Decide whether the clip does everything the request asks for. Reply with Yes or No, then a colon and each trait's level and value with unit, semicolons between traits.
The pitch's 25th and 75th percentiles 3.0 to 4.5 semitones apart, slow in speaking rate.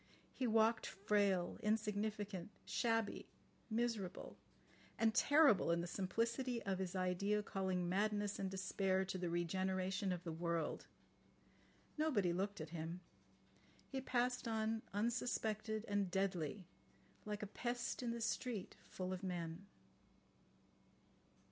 Yes: average, 3.3 semitones; slow, 115 wpm